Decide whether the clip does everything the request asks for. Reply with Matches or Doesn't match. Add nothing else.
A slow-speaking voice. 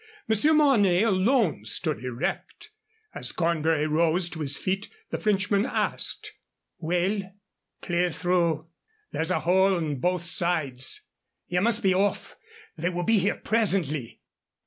Matches